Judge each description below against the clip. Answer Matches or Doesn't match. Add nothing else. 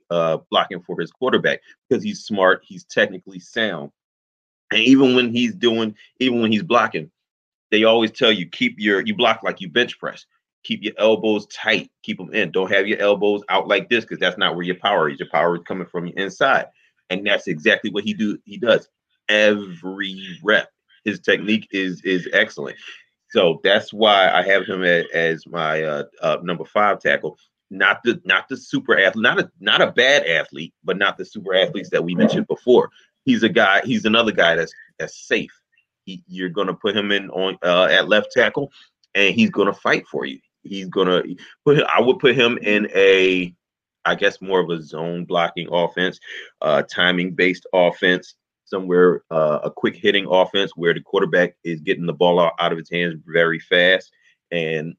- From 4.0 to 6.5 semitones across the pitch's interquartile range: Doesn't match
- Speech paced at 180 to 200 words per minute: Matches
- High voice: Doesn't match